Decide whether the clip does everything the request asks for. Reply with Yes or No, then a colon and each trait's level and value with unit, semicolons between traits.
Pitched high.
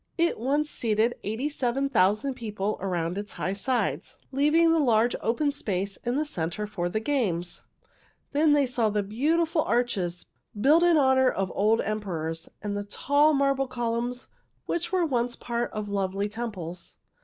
Yes: high, 235 Hz